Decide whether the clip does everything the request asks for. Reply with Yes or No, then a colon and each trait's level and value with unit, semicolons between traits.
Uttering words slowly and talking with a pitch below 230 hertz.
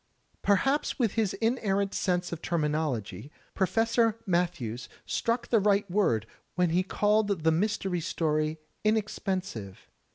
Yes: slow, 120 wpm; high, 190 Hz